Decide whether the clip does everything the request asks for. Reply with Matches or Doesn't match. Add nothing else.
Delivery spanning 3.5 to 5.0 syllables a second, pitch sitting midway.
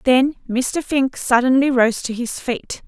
Doesn't match